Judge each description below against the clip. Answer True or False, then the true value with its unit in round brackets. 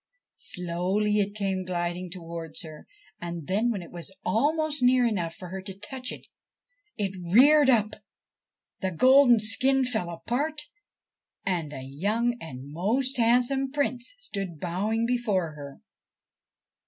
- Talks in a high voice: True (205 Hz)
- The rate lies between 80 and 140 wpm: True (135 wpm)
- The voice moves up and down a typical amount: False (6.1 semitones)